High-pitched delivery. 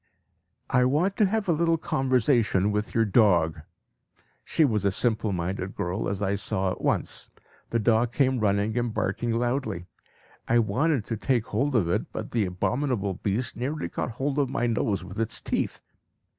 No: low, 115 Hz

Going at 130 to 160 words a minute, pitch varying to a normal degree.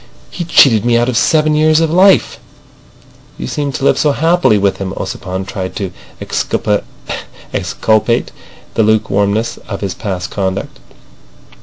No: average, 140 wpm; wide, 7.5 semitones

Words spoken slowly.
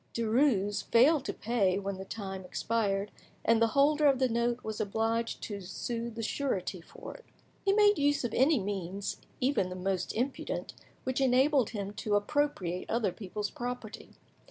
No: average, 165 wpm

